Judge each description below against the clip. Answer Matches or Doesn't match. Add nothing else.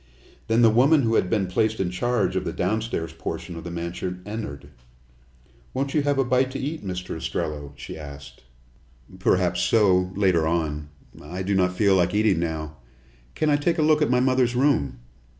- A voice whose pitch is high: Doesn't match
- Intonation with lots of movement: Matches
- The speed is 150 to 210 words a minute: Matches